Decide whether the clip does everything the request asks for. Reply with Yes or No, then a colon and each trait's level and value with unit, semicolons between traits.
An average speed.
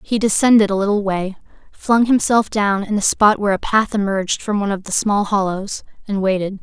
No: fast, 210 wpm